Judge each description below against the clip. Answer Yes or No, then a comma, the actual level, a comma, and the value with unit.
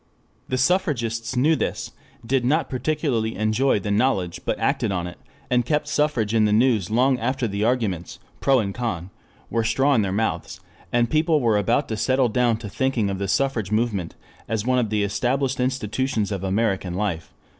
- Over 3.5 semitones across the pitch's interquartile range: Yes, average, 4.2 semitones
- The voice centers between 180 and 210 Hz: No, low, 115 Hz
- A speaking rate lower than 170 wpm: No, average, 185 wpm